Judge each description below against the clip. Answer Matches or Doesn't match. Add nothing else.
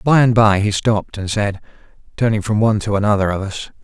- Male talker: Matches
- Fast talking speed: Matches